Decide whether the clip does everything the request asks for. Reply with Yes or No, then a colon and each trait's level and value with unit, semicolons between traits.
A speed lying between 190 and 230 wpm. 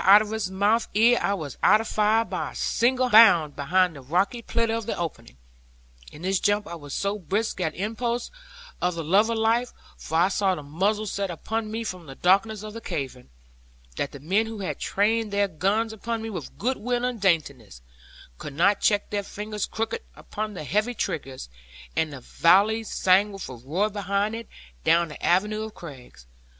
Yes: average, 195 wpm